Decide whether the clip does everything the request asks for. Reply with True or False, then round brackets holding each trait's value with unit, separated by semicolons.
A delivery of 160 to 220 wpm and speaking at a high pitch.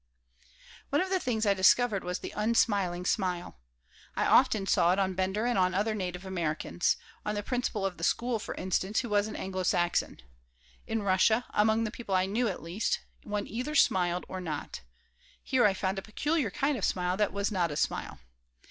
True (195 wpm; 200 Hz)